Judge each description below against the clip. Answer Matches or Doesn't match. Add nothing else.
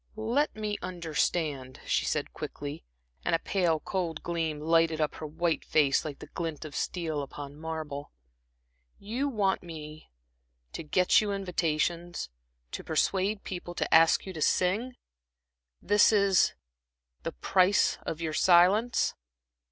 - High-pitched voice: Doesn't match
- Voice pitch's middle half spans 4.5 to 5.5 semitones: Doesn't match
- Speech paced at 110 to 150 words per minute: Matches